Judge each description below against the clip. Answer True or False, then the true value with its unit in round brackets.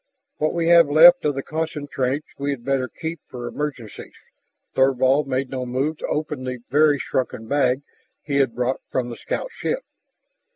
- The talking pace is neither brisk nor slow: True (165 wpm)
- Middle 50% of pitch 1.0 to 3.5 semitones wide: True (2.8 semitones)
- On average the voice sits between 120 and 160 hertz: True (140 Hz)